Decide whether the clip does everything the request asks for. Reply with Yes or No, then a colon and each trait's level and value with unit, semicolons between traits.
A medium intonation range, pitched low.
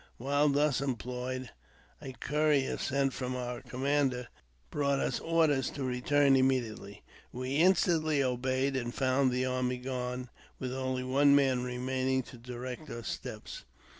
No: narrow, 1.8 semitones; low, 130 Hz